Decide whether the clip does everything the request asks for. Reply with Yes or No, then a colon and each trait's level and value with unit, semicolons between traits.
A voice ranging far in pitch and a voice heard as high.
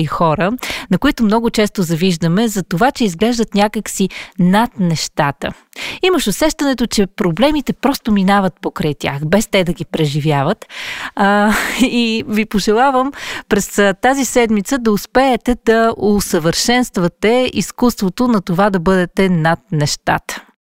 No: average, 4.6 semitones; high, 210 Hz